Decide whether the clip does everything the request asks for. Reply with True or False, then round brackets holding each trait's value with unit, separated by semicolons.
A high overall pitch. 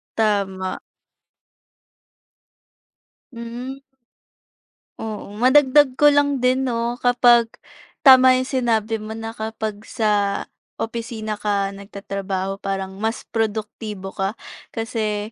True (220 Hz)